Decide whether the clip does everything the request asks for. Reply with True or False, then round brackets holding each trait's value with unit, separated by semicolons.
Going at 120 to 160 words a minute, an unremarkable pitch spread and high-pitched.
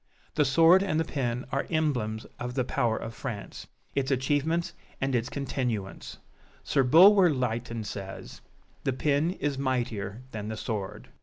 False (150 wpm; 4.4 semitones; 130 Hz)